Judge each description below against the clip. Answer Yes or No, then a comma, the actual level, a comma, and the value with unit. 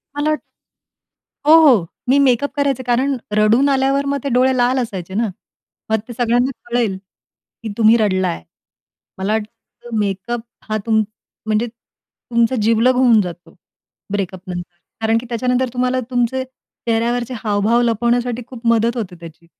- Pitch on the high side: Yes, high, 235 Hz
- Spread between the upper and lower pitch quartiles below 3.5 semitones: Yes, average, 2.9 semitones